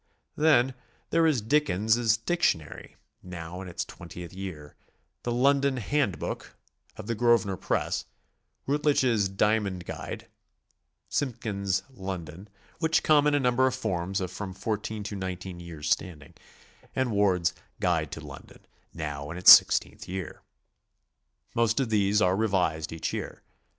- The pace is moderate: Yes, average, 145 wpm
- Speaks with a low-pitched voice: Yes, low, 100 Hz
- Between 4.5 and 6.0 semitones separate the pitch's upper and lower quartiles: Yes, average, 5.2 semitones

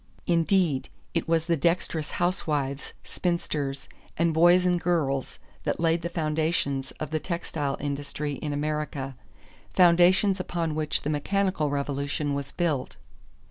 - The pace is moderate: No, slow, 130 wpm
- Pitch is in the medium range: Yes, medium, 155 Hz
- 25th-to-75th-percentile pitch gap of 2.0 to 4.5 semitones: Yes, average, 3.2 semitones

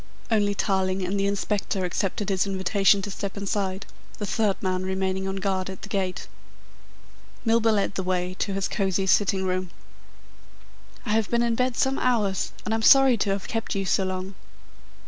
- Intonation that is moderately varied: No, narrow, 1.8 semitones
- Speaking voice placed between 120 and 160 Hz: No, high, 195 Hz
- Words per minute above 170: Yes, average, 180 wpm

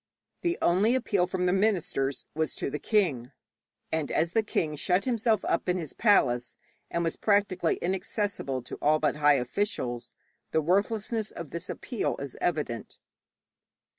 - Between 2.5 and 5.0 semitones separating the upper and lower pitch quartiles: No, wide, 5.6 semitones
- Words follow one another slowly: No, average, 155 wpm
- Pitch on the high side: No, medium, 175 Hz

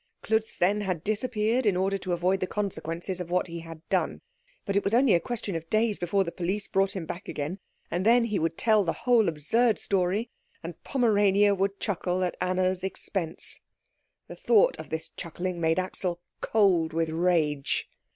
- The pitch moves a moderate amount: Yes, average, 3.4 semitones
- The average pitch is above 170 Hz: Yes, medium, 185 Hz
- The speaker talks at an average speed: Yes, average, 185 wpm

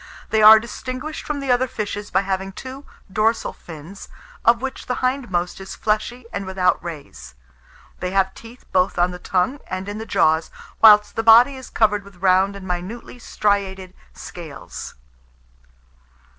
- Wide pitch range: No, average, 4.2 semitones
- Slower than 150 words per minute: No, average, 155 wpm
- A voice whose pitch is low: No, high, 200 Hz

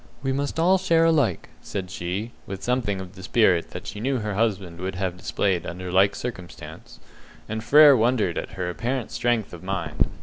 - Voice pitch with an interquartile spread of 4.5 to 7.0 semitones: Yes, average, 5.1 semitones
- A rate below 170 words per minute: No, average, 190 wpm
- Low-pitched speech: Yes, low, 105 Hz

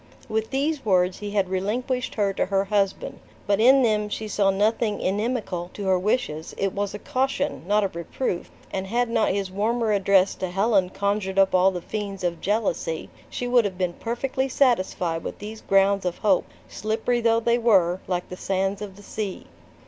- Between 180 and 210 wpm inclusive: Yes, average, 190 wpm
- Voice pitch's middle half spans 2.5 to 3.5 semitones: Yes, average, 3.2 semitones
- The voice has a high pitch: Yes, high, 200 Hz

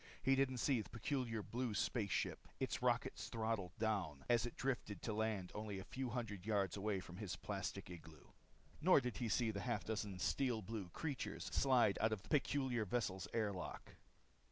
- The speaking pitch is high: No, low, 110 Hz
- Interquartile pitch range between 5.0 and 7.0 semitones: No, average, 3.9 semitones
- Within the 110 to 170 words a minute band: No, average, 180 wpm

